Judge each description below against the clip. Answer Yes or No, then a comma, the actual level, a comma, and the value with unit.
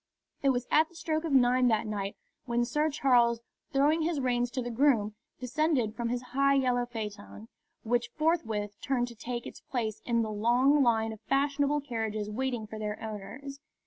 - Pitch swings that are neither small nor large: Yes, average, 3.9 semitones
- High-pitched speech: Yes, high, 245 Hz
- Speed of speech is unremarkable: Yes, average, 180 wpm